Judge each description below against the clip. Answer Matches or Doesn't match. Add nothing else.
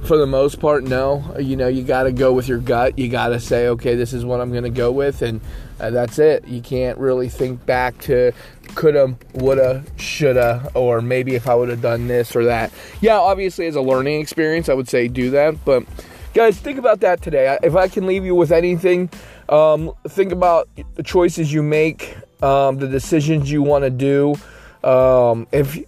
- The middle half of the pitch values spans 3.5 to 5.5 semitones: Matches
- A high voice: Doesn't match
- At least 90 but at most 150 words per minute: Doesn't match